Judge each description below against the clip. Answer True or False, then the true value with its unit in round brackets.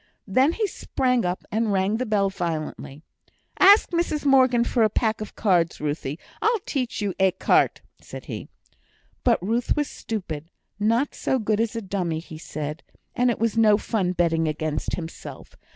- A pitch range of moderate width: False (6.0 semitones)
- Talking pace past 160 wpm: True (170 wpm)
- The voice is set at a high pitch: True (210 Hz)